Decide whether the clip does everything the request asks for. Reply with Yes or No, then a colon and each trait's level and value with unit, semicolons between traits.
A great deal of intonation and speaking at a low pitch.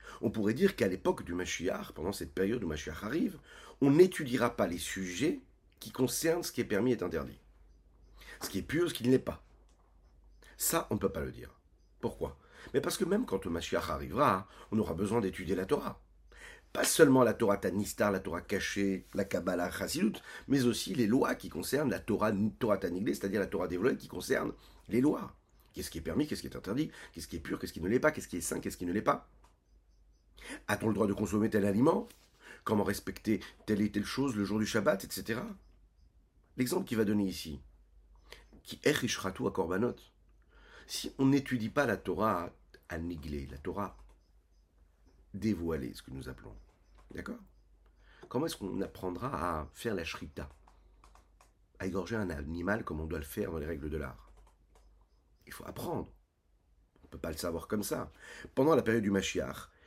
Yes: wide, 6.6 semitones; very low, 95 Hz